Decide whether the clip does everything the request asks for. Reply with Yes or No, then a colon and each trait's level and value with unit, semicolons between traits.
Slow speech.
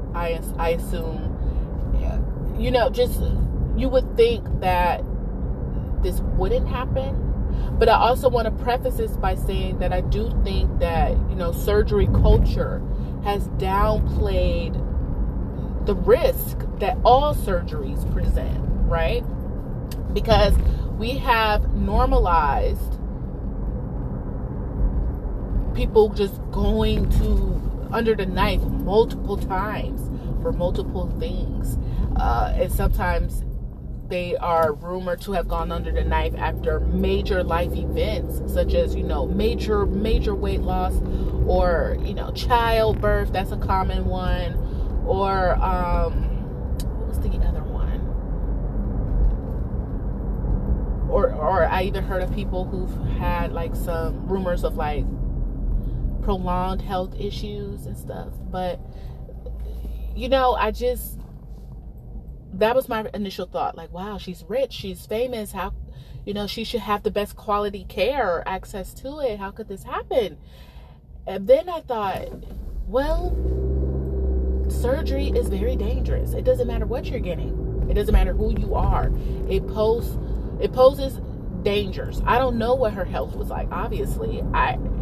Yes: slow, 130 wpm